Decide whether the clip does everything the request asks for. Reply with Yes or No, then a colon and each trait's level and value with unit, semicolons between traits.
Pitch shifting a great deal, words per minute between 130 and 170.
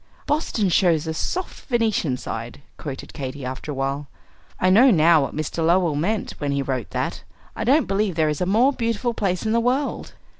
No: wide, 7.7 semitones; average, 195 wpm